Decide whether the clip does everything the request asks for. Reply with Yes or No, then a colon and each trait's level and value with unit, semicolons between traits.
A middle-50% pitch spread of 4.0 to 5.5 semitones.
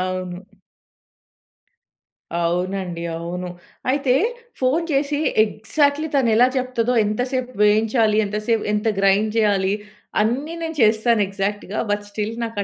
Yes: average, 4.3 semitones